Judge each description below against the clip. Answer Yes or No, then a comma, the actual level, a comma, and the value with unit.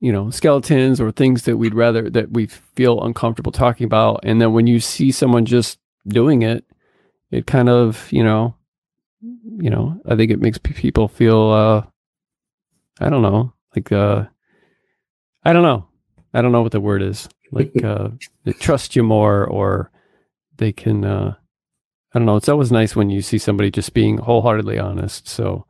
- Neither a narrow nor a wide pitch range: No, narrow, 2.3 semitones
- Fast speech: No, average, 180 wpm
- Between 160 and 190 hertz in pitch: No, low, 115 Hz